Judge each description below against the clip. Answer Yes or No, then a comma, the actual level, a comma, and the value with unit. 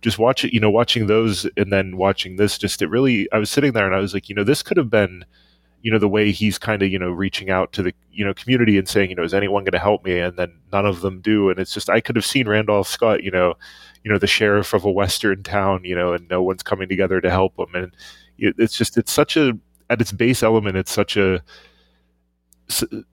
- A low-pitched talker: Yes, low, 100 Hz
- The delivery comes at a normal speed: No, fast, 265 wpm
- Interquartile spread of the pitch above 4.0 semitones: No, average, 2.7 semitones